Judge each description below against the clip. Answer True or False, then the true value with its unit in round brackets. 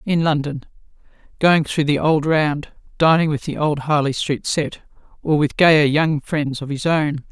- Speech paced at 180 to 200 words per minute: False (170 wpm)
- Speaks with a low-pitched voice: False (150 Hz)